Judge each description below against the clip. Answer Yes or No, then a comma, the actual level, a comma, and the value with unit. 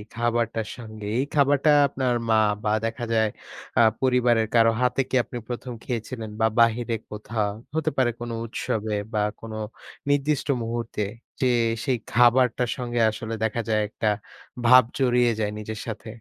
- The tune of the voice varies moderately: No, narrow, 2.2 semitones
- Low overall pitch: Yes, low, 120 Hz